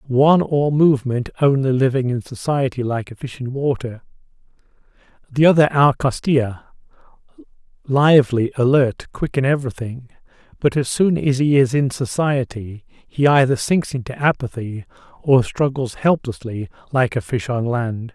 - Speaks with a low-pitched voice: Yes, low, 130 Hz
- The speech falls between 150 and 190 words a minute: No, average, 140 wpm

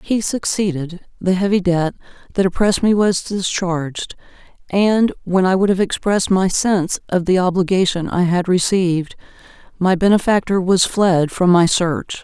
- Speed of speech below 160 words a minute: Yes, average, 150 wpm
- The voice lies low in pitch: No, medium, 185 Hz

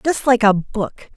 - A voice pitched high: Yes, high, 220 Hz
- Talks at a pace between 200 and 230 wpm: Yes, fast, 205 wpm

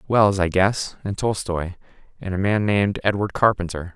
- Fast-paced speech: No, average, 165 wpm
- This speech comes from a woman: No, male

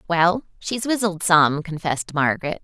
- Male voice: No, female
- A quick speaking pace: No, slow, 135 wpm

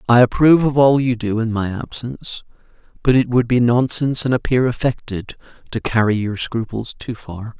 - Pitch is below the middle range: Yes, low, 120 Hz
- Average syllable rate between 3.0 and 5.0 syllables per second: No, 5.3 syllables/s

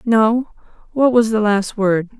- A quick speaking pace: No, average, 165 wpm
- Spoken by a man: No, female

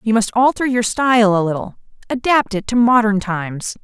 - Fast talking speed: No, average, 170 wpm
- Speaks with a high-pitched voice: Yes, high, 220 Hz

